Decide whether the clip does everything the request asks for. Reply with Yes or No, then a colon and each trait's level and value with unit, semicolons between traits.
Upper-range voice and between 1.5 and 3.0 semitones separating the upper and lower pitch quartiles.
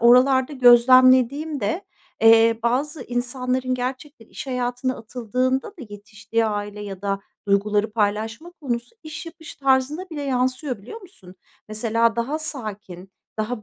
No: high, 245 Hz; average, 3.6 semitones